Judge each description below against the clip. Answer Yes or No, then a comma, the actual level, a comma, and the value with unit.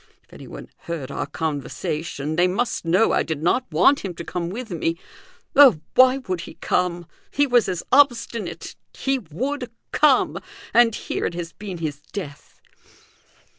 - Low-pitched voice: No, medium, 180 Hz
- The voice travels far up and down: Yes, wide, 6.8 semitones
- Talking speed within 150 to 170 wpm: Yes, average, 160 wpm